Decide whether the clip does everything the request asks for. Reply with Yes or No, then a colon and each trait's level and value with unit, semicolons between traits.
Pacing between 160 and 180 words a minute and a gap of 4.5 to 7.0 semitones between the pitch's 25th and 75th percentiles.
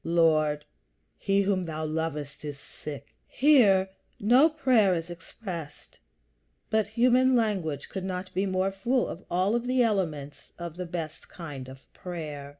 No: average, 145 wpm; wide, 5.4 semitones